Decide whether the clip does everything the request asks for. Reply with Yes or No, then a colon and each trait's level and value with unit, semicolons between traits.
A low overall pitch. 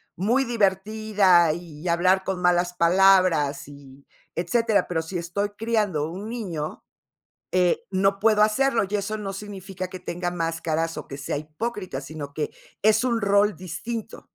No: medium, 185 Hz